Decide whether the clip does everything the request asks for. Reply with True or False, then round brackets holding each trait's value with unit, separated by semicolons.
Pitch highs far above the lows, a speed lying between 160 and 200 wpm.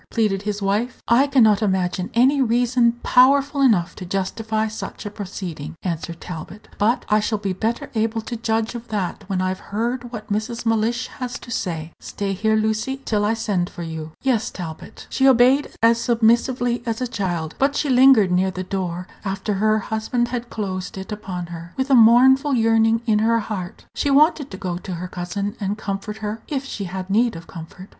False (4.0 semitones; 195 wpm)